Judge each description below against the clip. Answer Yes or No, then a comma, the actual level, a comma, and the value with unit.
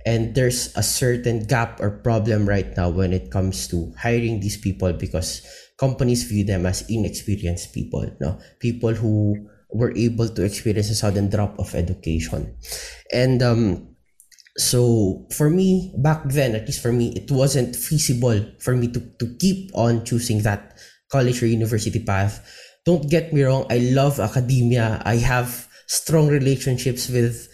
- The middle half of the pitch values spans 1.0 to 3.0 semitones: No, average, 3.6 semitones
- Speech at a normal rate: No, fast, 160 wpm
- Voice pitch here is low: Yes, low, 115 Hz